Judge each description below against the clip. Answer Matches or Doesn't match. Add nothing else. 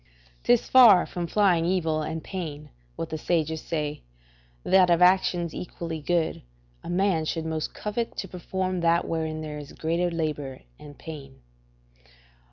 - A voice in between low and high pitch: Matches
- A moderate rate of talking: Matches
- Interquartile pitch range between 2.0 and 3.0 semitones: Matches